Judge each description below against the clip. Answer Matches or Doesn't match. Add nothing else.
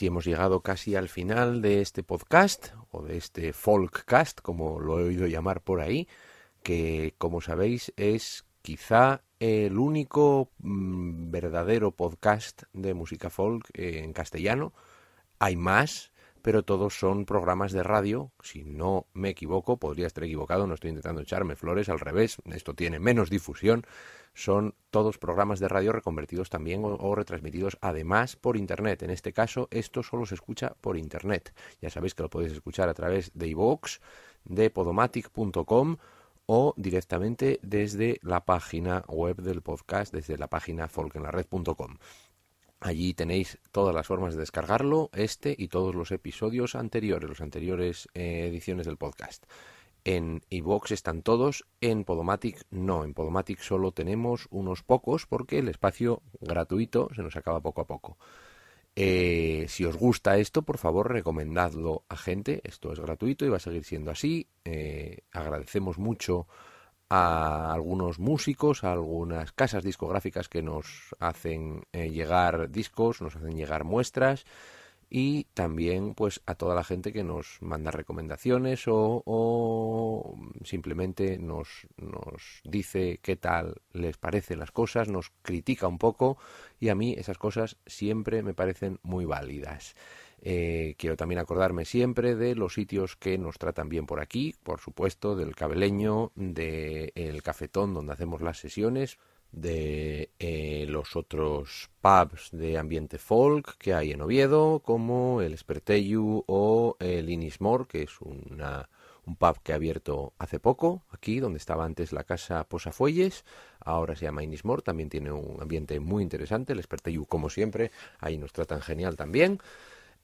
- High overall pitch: Doesn't match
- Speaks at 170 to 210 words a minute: Doesn't match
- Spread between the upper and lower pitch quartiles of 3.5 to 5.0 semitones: Matches